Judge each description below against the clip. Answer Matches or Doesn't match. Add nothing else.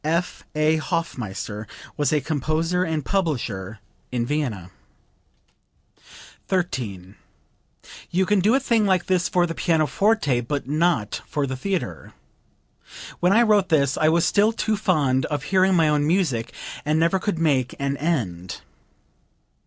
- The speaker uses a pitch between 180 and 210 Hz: Doesn't match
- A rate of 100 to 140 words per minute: Matches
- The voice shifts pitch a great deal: Matches